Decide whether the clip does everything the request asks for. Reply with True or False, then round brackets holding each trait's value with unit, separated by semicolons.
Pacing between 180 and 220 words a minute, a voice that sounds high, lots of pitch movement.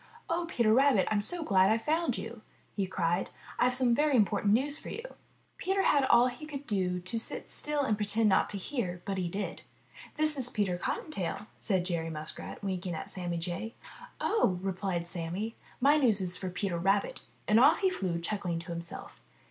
True (190 wpm; 205 Hz; 6.5 semitones)